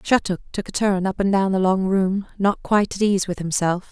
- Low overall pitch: No, high, 190 Hz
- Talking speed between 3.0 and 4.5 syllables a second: No, 5.3 syllables/s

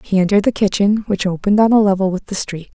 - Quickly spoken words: Yes, fast, 260 wpm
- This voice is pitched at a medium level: No, high, 200 Hz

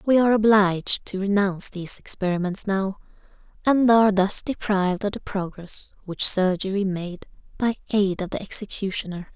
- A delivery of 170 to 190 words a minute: No, average, 150 wpm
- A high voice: Yes, high, 195 Hz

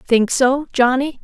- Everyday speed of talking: Yes, average, 145 wpm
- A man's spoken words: No, female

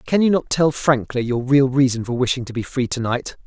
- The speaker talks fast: Yes, fast, 260 wpm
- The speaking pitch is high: No, low, 130 Hz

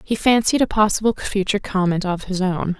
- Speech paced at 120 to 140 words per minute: No, average, 195 wpm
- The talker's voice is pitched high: Yes, high, 200 Hz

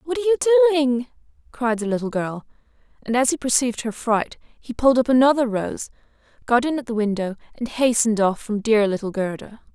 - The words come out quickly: No, average, 190 wpm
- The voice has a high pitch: Yes, high, 245 Hz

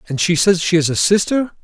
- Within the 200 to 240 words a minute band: No, fast, 255 wpm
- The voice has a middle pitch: Yes, medium, 180 Hz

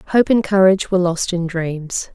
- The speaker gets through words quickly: No, average, 195 wpm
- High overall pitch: No, medium, 180 Hz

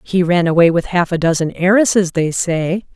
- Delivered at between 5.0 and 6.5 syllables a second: Yes, 5.1 syllables/s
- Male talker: No, female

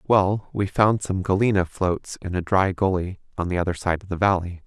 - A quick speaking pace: Yes, fast, 220 wpm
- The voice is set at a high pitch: No, very low, 95 Hz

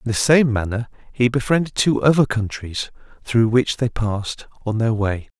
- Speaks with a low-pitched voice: Yes, low, 115 Hz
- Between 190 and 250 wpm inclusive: No, average, 180 wpm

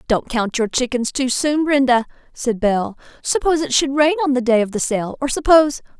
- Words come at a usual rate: No, fast, 210 wpm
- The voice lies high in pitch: Yes, very high, 255 Hz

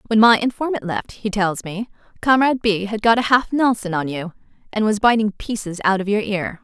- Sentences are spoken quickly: Yes, fast, 215 wpm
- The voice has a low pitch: No, high, 210 Hz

